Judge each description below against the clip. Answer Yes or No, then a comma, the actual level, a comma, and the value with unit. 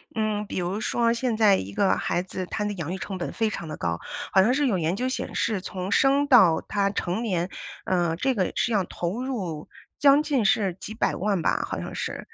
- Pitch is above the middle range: Yes, high, 200 Hz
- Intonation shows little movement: No, average, 4.4 semitones